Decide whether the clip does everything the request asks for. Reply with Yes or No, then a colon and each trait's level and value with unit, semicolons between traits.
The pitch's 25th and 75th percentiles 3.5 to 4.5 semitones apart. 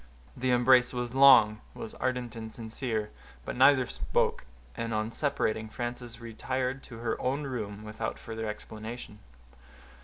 No: narrow, 2.6 semitones